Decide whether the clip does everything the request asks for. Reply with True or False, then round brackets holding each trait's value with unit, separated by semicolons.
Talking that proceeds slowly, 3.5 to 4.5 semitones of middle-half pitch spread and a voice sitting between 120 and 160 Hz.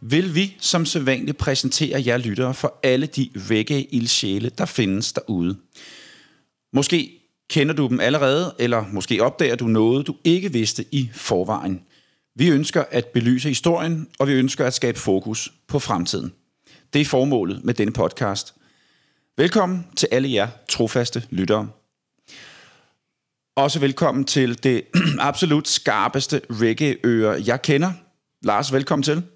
True (135 wpm; 4.2 semitones; 135 Hz)